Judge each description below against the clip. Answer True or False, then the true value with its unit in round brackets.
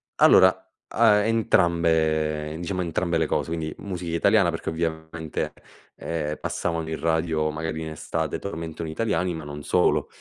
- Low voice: True (80 Hz)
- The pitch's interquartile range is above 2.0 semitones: False (1.6 semitones)